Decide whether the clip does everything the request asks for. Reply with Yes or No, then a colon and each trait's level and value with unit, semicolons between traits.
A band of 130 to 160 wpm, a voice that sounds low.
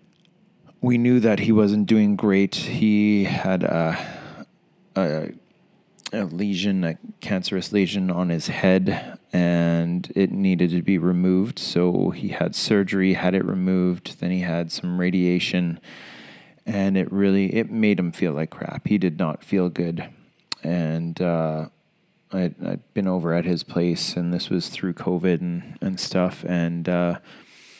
Yes: average, 155 wpm; very low, 90 Hz